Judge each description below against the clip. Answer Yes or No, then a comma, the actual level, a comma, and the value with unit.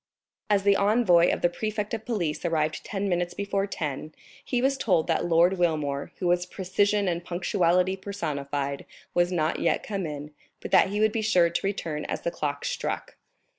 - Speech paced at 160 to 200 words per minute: Yes, average, 185 wpm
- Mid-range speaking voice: Yes, medium, 180 Hz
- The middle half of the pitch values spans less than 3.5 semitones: No, average, 3.8 semitones